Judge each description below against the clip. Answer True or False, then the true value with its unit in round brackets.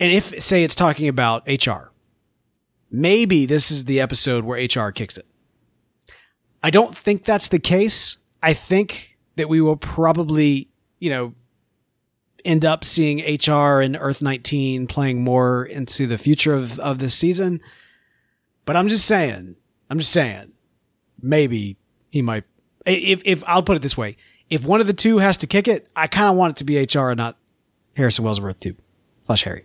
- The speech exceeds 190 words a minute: False (180 wpm)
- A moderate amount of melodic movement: False (5.9 semitones)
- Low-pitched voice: False (145 Hz)